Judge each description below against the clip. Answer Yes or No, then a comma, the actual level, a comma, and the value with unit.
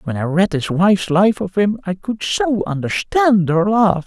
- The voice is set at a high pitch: Yes, high, 195 Hz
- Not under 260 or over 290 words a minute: No, fast, 205 wpm